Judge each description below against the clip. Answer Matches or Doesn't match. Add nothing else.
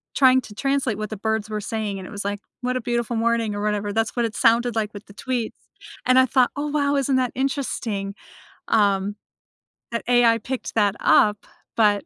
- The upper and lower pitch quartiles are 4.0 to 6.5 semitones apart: Doesn't match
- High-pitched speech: Matches